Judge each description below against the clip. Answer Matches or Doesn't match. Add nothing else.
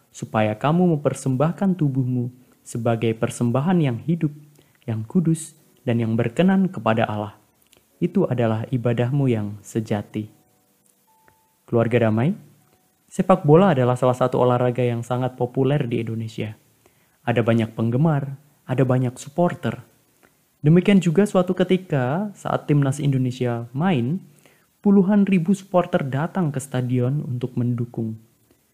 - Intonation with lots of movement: Matches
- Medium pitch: Doesn't match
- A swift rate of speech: Doesn't match